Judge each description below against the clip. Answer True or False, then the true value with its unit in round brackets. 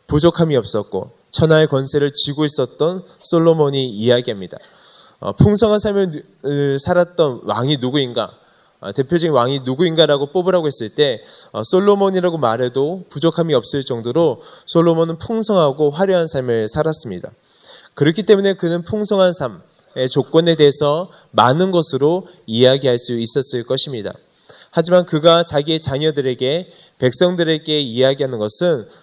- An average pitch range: True (4.8 semitones)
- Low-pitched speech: False (155 Hz)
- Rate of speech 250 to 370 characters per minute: True (325 characters per minute)